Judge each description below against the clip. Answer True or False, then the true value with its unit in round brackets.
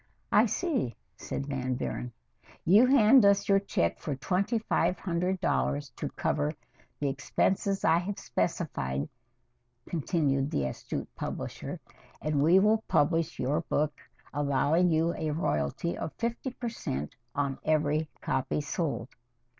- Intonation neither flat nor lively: False (5.7 semitones)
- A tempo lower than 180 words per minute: True (135 wpm)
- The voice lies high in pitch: False (155 Hz)